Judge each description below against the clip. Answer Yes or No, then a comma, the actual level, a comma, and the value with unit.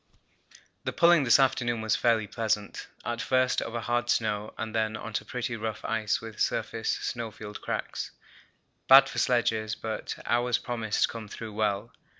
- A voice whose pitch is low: Yes, low, 115 Hz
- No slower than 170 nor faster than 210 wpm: No, average, 160 wpm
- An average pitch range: No, narrow, 1.8 semitones